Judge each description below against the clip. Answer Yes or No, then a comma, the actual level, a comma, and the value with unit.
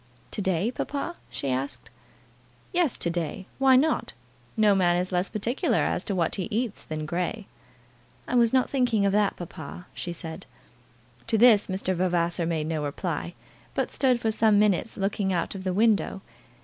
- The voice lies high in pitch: Yes, high, 195 Hz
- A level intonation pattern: No, average, 4.5 semitones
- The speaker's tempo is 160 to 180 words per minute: Yes, average, 175 wpm